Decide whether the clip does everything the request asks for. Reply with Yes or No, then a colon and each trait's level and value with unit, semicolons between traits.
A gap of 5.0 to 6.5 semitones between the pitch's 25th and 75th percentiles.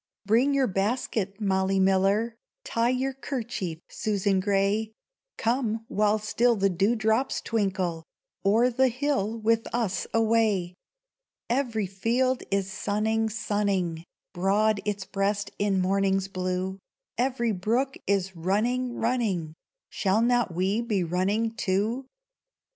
No: average, 3.2 semitones